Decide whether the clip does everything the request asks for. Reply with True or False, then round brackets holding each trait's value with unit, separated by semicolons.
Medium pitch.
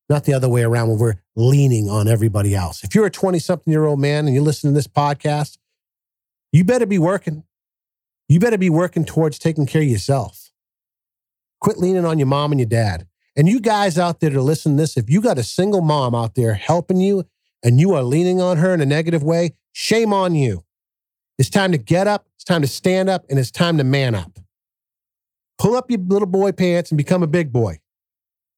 True (150 Hz)